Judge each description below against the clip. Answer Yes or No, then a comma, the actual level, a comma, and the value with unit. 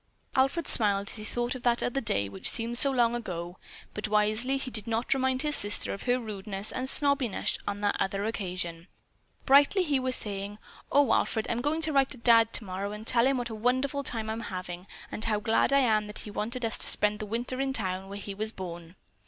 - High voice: Yes, high, 225 Hz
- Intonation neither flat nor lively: Yes, average, 4.0 semitones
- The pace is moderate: No, fast, 225 wpm